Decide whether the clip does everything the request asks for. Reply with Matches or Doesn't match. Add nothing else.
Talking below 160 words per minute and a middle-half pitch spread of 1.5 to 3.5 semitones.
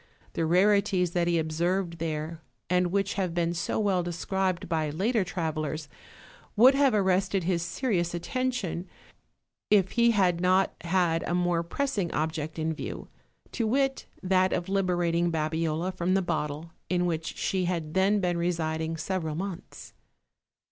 Matches